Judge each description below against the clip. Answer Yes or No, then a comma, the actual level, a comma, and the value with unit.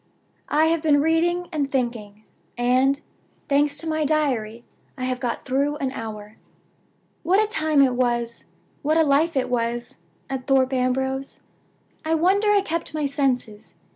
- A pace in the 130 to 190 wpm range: Yes, average, 155 wpm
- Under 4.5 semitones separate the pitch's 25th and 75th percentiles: Yes, average, 4.0 semitones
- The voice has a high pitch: Yes, very high, 275 Hz